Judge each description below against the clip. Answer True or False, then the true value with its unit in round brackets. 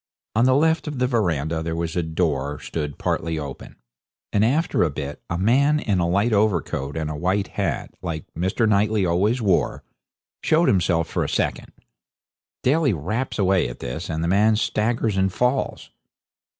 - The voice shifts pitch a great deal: True (5.8 semitones)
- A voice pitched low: True (95 Hz)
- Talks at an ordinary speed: True (175 wpm)